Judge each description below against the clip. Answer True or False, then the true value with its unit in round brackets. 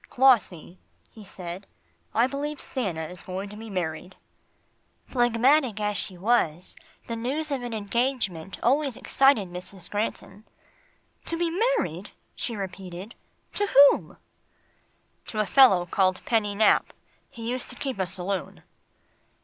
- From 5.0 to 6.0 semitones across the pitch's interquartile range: True (5.4 semitones)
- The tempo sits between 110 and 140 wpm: True (135 wpm)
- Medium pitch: False (210 Hz)